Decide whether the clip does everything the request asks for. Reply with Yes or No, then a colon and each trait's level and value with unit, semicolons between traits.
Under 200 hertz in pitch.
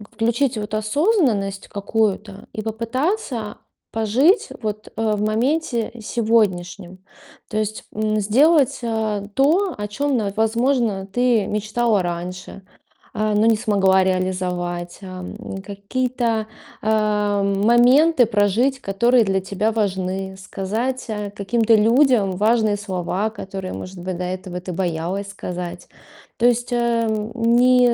No: high, 215 Hz